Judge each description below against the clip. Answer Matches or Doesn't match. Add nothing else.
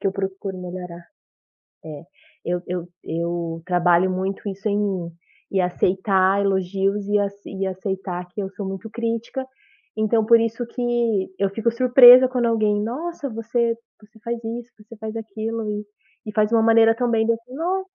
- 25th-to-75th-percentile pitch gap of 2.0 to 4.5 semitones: Matches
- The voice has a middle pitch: Doesn't match